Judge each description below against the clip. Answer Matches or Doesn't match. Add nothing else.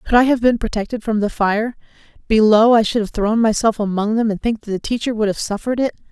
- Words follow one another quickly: Matches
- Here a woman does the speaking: Matches